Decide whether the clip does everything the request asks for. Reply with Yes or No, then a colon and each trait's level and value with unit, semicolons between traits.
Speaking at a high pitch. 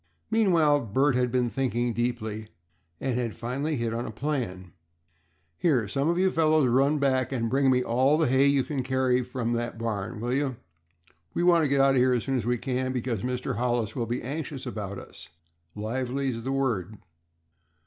No: low, 125 Hz